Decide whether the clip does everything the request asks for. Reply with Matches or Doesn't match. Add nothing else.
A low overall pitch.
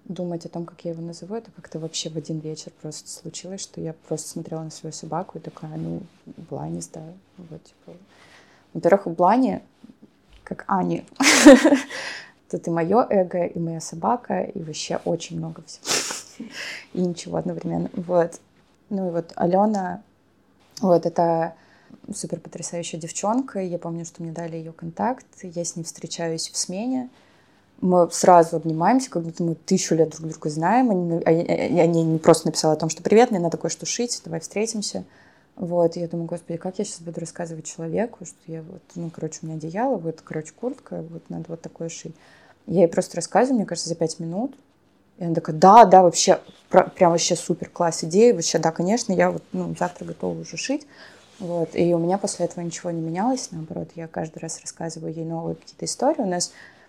Doesn't match